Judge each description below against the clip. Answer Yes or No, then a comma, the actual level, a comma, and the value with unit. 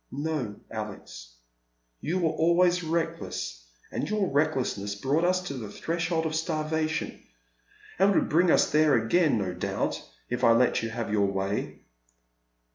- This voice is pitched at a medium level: Yes, medium, 150 Hz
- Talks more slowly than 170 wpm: Yes, average, 155 wpm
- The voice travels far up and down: Yes, wide, 7.4 semitones